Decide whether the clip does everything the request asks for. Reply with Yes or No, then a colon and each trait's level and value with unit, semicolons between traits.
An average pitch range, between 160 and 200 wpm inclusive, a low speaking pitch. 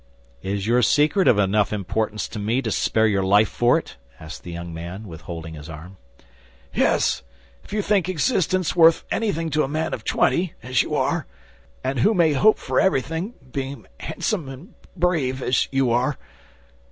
No: wide, 8.2 semitones; average, 175 wpm; low, 130 Hz